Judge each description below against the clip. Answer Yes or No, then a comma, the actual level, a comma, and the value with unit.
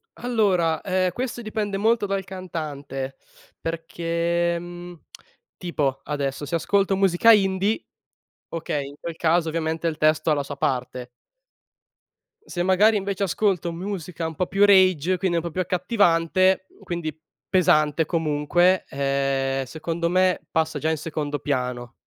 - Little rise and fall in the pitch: No, average, 3.6 semitones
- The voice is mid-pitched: Yes, medium, 170 Hz